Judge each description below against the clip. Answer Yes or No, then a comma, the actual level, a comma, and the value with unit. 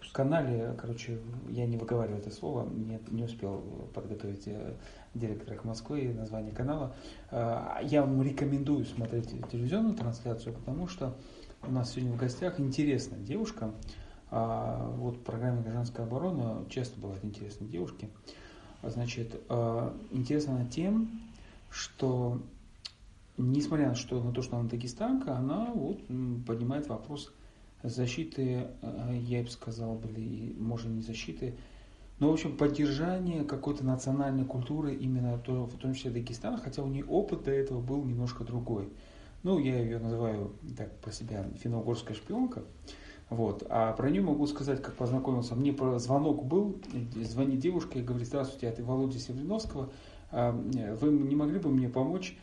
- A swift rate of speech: No, average, 135 wpm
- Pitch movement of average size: Yes, average, 3.2 semitones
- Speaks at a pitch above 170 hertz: No, low, 120 Hz